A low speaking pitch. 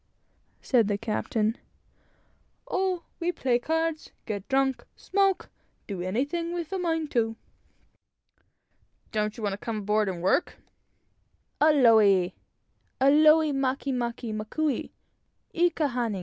No: very high, 250 Hz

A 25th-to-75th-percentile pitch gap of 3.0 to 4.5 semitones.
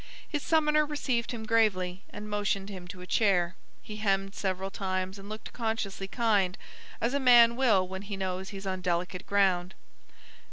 Yes: average, 3.3 semitones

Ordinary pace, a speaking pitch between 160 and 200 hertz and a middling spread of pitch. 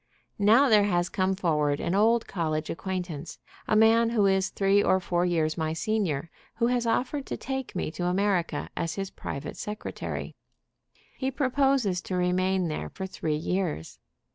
Yes: average, 165 wpm; high, 190 Hz; average, 4.4 semitones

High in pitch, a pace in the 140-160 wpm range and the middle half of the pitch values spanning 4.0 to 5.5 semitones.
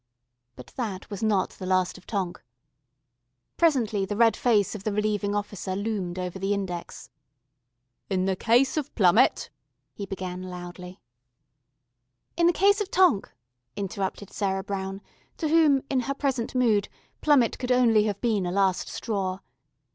Yes: high, 205 Hz; average, 155 wpm; average, 4.4 semitones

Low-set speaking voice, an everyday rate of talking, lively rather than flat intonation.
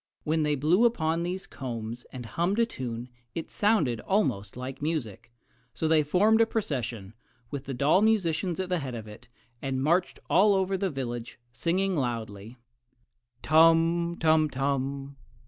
No: medium, 150 Hz; average, 155 wpm; wide, 6.3 semitones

